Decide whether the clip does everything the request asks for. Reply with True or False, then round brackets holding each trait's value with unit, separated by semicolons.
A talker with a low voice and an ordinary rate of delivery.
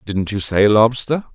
True (110 Hz; 180 wpm)